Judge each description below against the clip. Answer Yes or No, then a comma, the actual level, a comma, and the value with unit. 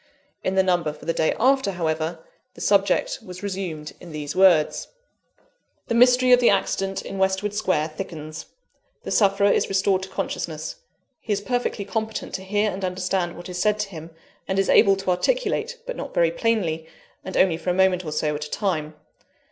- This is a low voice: No, high, 190 Hz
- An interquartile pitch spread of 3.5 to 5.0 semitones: Yes, average, 3.8 semitones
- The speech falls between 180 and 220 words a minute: Yes, average, 190 wpm